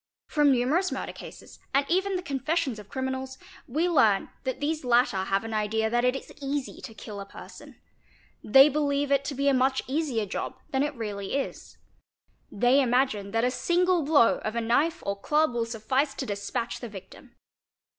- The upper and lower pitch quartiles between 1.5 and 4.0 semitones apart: No, average, 4.4 semitones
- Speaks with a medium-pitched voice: No, very high, 260 Hz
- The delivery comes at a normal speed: Yes, average, 185 wpm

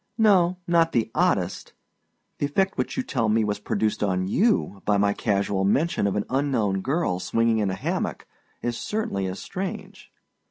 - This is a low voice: Yes, low, 115 Hz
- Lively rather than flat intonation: Yes, wide, 8.9 semitones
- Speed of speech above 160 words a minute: Yes, average, 170 wpm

